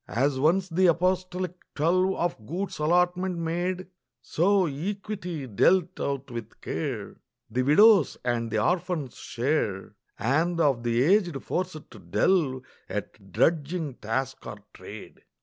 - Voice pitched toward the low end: No, medium, 165 Hz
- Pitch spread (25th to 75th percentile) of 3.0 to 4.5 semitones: No, average, 5.2 semitones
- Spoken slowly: Yes, slow, 130 wpm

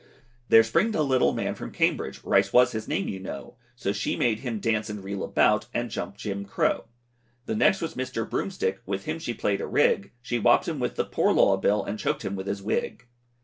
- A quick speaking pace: Yes, fast, 225 wpm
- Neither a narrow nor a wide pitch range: Yes, average, 3.8 semitones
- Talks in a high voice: No, low, 105 Hz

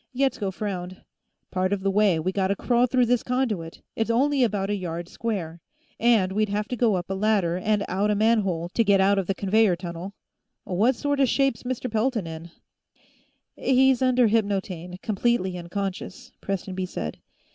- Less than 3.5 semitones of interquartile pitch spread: No, average, 4.1 semitones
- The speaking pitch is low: No, high, 200 Hz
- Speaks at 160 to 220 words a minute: Yes, average, 170 wpm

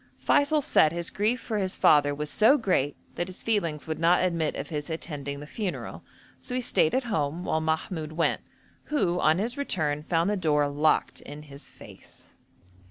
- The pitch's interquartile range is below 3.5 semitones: No, average, 5.3 semitones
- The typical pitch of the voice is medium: Yes, medium, 165 Hz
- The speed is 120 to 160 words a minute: No, average, 185 wpm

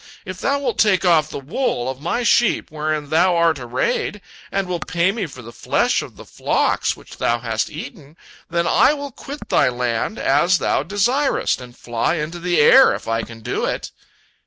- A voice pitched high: No, medium, 170 Hz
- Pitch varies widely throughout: Yes, wide, 7.1 semitones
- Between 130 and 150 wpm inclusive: No, average, 195 wpm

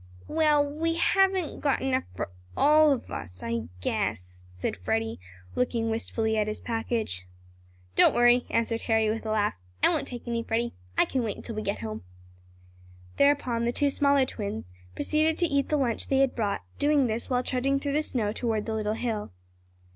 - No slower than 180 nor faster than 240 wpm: Yes, average, 185 wpm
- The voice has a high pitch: Yes, high, 235 Hz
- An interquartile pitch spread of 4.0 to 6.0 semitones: Yes, average, 4.6 semitones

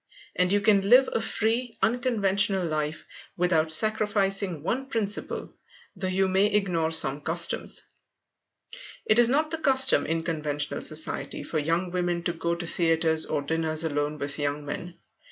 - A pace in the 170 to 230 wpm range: No, average, 155 wpm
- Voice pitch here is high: No, medium, 175 Hz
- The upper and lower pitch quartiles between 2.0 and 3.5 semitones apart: No, average, 4.6 semitones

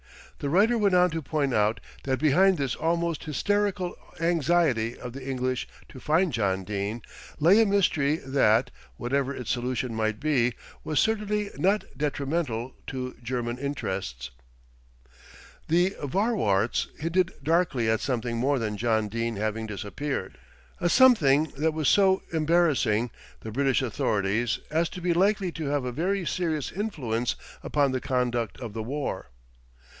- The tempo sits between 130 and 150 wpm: Yes, average, 145 wpm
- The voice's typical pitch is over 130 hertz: Yes, medium, 140 Hz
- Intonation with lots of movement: Yes, wide, 6.5 semitones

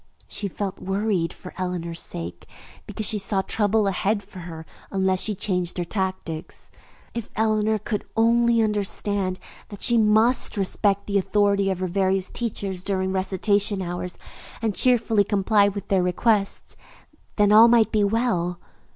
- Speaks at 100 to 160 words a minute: Yes, average, 150 wpm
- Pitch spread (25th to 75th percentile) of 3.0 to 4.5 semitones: No, narrow, 2.4 semitones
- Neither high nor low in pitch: No, high, 200 Hz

